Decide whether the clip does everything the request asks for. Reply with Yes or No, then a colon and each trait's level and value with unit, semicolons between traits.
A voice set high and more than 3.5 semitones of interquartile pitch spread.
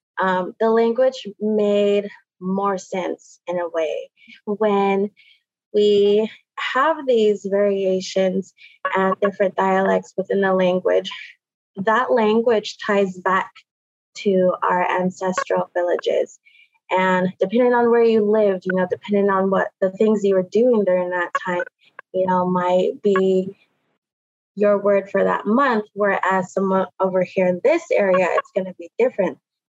No: high, 195 Hz; average, 2.7 semitones